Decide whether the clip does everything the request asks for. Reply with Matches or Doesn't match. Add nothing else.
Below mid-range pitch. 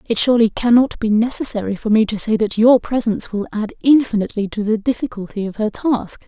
Doesn't match